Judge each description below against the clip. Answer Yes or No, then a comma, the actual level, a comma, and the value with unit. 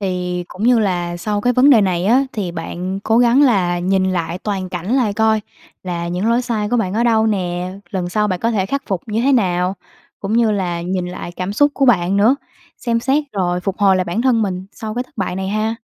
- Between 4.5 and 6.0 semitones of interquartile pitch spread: No, average, 4.0 semitones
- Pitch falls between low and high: No, high, 200 Hz